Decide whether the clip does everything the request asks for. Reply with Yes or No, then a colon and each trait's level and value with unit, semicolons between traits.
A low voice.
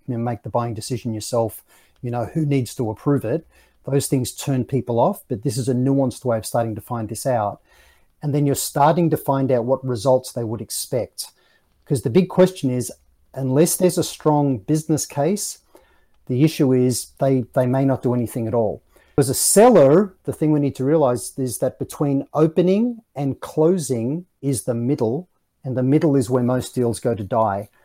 Yes: low, 130 Hz